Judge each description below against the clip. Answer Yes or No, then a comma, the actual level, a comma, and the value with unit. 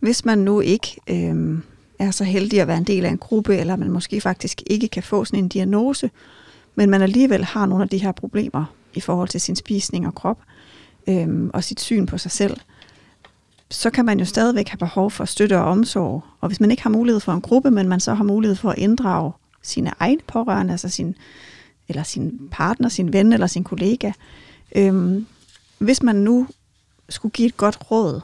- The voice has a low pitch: No, high, 200 Hz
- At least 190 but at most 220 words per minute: Yes, average, 210 wpm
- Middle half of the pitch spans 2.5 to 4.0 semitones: Yes, average, 3.3 semitones